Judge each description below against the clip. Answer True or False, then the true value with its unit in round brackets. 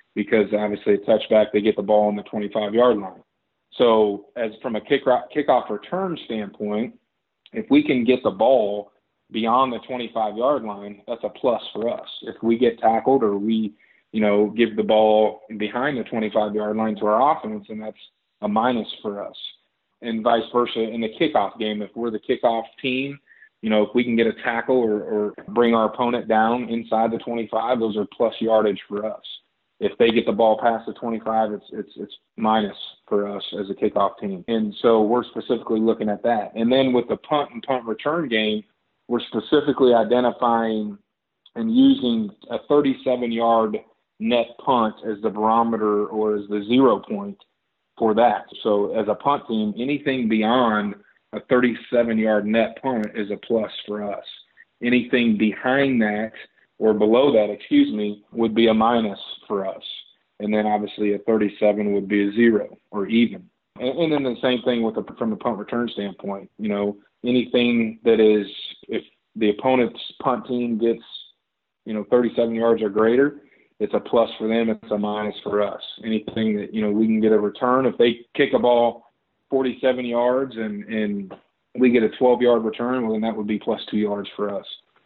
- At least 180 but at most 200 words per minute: True (185 wpm)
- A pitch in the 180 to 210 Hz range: False (115 Hz)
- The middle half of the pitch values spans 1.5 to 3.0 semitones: True (2.4 semitones)